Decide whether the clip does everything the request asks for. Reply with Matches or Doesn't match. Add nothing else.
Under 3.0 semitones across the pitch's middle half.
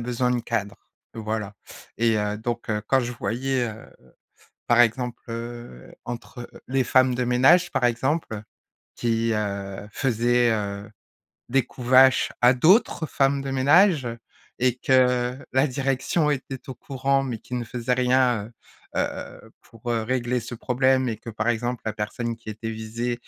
Matches